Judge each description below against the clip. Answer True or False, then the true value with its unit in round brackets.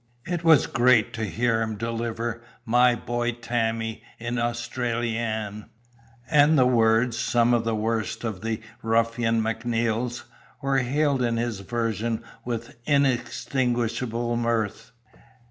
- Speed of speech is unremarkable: False (120 wpm)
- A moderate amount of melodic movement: False (1.3 semitones)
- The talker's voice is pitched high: False (115 Hz)